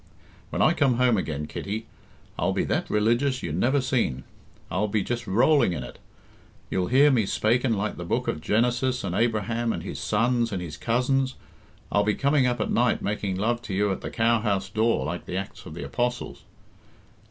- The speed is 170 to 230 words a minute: Yes, average, 195 wpm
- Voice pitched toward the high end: No, low, 115 Hz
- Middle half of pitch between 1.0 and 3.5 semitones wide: No, average, 4.0 semitones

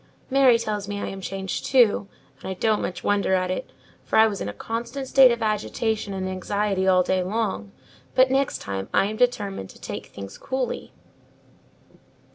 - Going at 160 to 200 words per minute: Yes, average, 185 wpm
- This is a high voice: Yes, high, 205 Hz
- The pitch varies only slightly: No, average, 3.7 semitones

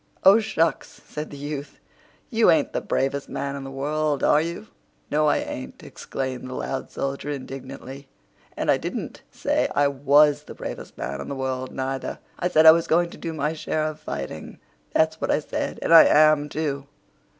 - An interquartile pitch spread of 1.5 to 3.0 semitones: Yes, narrow, 2.5 semitones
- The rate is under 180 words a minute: No, average, 185 wpm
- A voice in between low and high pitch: Yes, medium, 145 Hz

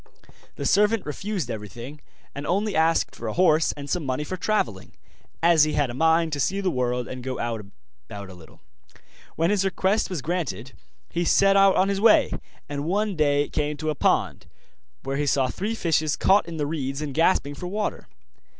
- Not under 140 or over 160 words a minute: No, average, 195 wpm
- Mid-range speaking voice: Yes, medium, 155 Hz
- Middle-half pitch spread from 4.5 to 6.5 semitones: Yes, wide, 5.5 semitones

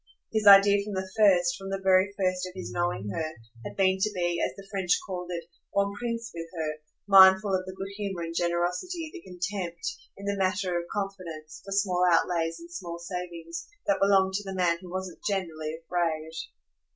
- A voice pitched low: No, medium, 185 Hz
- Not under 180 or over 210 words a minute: Yes, average, 195 wpm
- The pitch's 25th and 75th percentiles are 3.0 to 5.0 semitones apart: No, narrow, 2.4 semitones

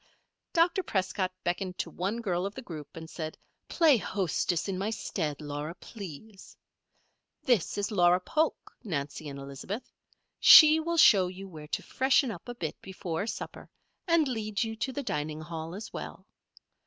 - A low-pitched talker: No, high, 190 Hz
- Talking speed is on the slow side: No, average, 165 wpm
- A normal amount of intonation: No, wide, 6.2 semitones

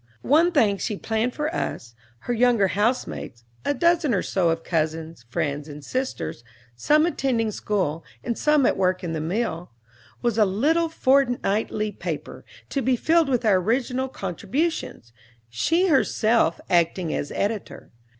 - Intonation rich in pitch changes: Yes, wide, 7.6 semitones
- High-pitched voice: Yes, high, 220 Hz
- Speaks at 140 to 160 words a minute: Yes, average, 150 wpm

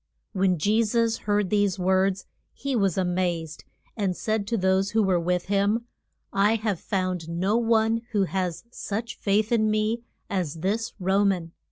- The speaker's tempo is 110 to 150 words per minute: No, average, 175 wpm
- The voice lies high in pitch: Yes, high, 200 Hz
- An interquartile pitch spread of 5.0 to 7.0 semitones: No, average, 2.9 semitones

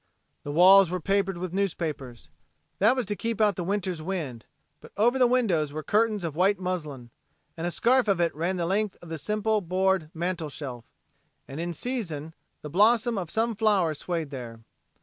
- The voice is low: No, medium, 185 Hz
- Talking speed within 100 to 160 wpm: No, average, 190 wpm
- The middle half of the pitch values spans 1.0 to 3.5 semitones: No, average, 4.8 semitones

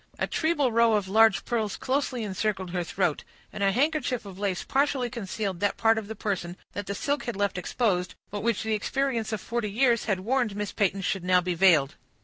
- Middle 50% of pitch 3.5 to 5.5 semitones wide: Yes, average, 3.8 semitones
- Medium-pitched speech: No, high, 210 Hz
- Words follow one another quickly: Yes, fast, 210 wpm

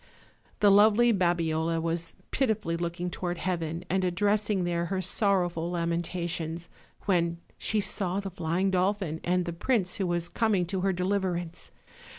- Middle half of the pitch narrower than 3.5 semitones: Yes, narrow, 2.5 semitones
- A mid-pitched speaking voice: Yes, medium, 180 Hz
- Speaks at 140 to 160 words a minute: Yes, average, 150 wpm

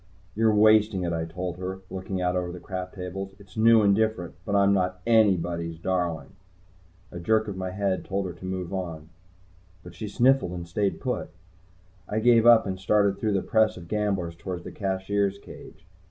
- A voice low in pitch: Yes, very low, 95 Hz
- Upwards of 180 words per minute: Yes, average, 190 wpm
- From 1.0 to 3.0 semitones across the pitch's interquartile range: Yes, average, 2.7 semitones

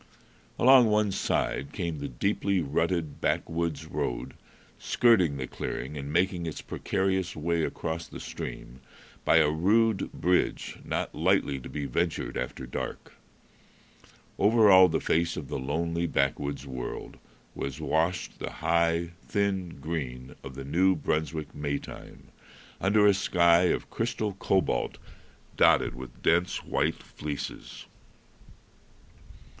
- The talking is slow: Yes, slow, 130 wpm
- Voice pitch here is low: Yes, very low, 85 Hz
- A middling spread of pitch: Yes, average, 4.7 semitones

